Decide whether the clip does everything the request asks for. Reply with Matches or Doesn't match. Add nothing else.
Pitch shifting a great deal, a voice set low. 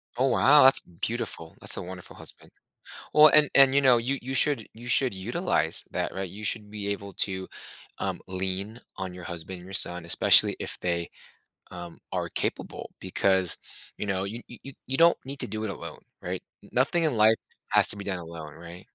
Matches